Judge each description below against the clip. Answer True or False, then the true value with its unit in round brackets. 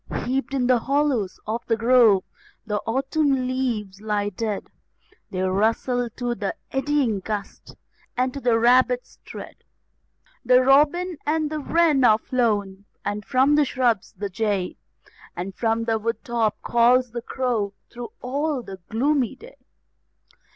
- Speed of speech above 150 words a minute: False (145 wpm)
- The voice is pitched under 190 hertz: False (240 Hz)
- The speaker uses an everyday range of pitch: True (3.9 semitones)